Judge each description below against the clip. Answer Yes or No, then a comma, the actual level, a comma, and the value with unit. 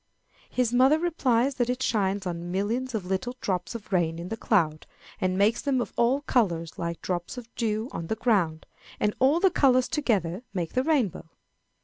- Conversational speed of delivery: Yes, average, 190 wpm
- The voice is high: Yes, high, 220 Hz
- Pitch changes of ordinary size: No, wide, 5.8 semitones